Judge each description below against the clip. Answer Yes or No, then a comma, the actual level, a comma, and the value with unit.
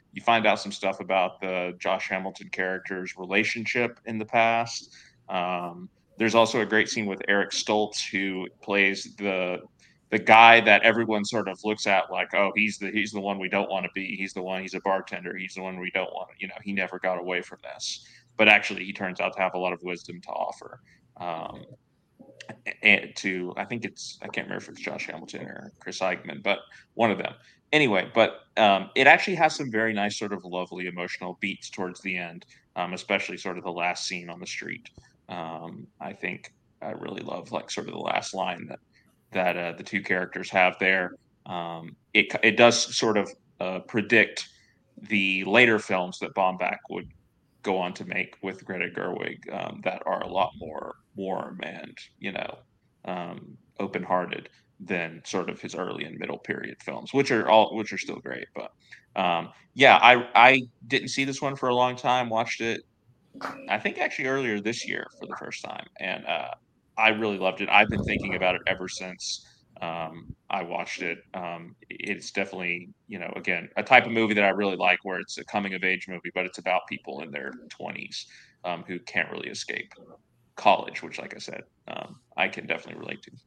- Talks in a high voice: No, very low, 95 Hz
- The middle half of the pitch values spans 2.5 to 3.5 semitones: Yes, average, 3.2 semitones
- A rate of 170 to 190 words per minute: No, average, 200 wpm